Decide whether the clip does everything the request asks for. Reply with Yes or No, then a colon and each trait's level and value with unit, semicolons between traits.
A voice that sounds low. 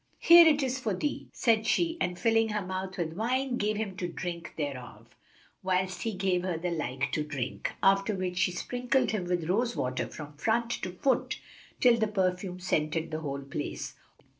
No: medium, 185 Hz